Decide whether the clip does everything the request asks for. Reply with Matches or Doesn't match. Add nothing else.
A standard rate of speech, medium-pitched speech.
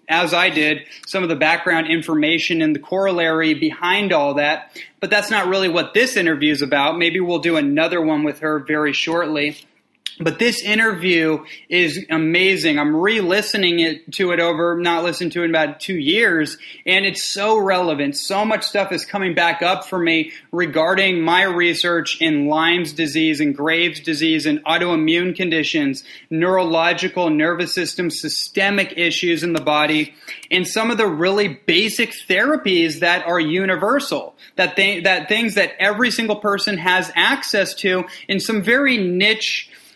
Matches